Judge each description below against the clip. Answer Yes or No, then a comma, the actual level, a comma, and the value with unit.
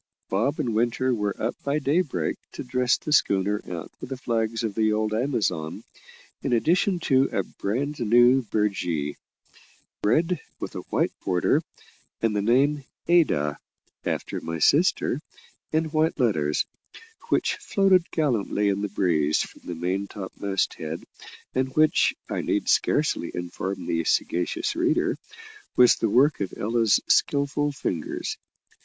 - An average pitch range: No, wide, 6.7 semitones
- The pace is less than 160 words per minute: Yes, average, 140 wpm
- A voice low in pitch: Yes, low, 115 Hz